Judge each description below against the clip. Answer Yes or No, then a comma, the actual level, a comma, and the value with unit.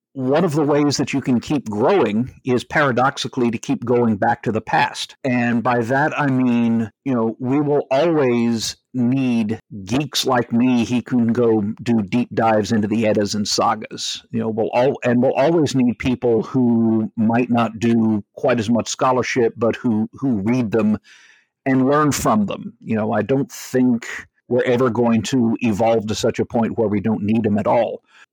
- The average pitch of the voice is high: No, low, 120 Hz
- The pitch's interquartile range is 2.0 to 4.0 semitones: Yes, narrow, 2.6 semitones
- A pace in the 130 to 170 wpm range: No, average, 190 wpm